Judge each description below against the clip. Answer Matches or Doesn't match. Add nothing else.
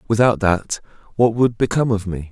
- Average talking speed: Matches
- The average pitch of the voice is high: Doesn't match